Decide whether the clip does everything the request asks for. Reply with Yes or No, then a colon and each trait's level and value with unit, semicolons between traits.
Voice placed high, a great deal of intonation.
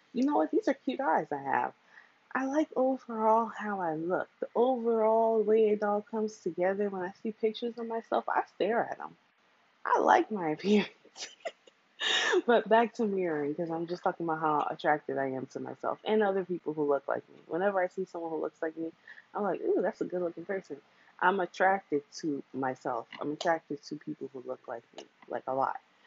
Yes: high, 195 Hz; wide, 5.9 semitones